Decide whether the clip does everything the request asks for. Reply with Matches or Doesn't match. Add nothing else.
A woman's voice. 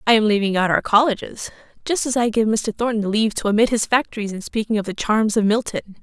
Matches